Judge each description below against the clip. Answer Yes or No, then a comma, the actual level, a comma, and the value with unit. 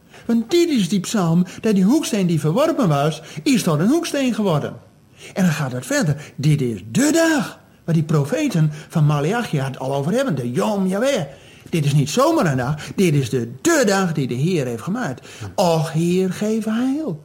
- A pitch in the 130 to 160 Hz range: No, medium, 170 Hz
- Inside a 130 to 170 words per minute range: No, fast, 200 wpm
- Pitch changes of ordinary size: No, wide, 7.0 semitones